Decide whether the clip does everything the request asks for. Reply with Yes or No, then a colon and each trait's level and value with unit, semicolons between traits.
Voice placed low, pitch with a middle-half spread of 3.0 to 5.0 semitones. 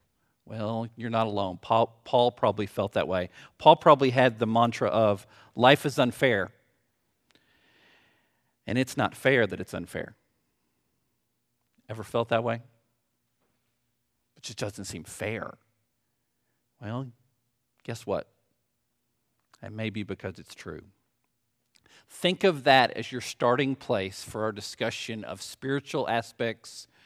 No: low, 115 Hz; narrow, 2.5 semitones